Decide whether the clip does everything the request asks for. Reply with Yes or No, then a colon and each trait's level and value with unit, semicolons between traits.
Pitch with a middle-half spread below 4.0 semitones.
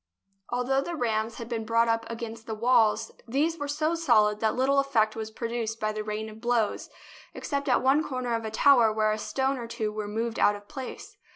Yes: average, 3.3 semitones